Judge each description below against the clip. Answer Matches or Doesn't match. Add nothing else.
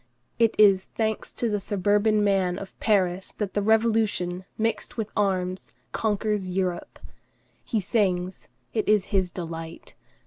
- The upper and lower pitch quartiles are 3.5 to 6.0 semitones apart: Doesn't match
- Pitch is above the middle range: Matches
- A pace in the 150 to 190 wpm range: Doesn't match